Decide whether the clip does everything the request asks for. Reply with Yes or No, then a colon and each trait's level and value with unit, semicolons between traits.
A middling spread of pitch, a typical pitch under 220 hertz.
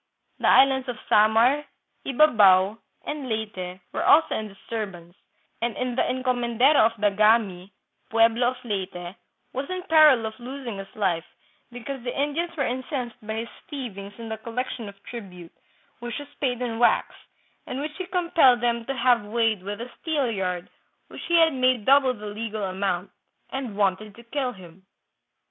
No: average, 4.2 semitones; high, 235 Hz